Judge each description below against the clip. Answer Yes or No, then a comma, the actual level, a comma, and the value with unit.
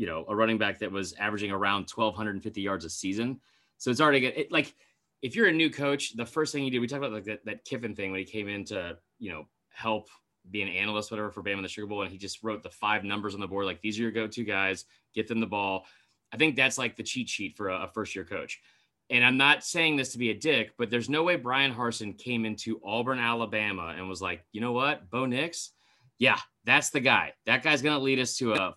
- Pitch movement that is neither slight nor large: Yes, average, 3.9 semitones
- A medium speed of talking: No, fast, 265 wpm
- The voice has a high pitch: No, low, 110 Hz